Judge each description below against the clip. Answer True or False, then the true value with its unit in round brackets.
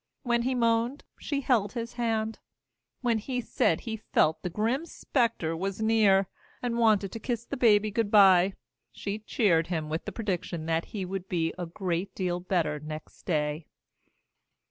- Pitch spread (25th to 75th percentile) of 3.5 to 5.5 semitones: True (4.8 semitones)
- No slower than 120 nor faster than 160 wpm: False (170 wpm)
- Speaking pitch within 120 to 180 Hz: False (205 Hz)